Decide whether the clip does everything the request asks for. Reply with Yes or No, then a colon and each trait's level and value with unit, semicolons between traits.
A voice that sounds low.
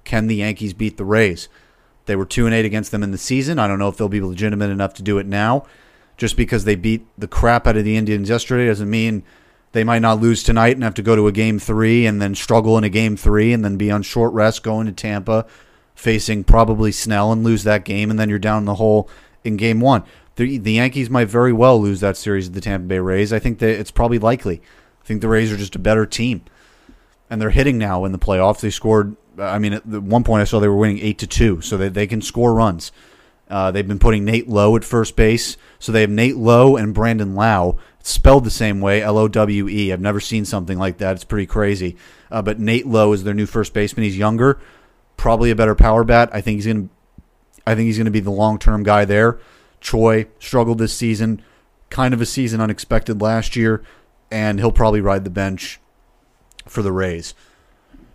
Yes: low, 110 Hz